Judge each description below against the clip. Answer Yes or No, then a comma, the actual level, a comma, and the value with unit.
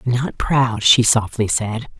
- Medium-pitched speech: No, low, 115 Hz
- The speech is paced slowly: No, average, 150 wpm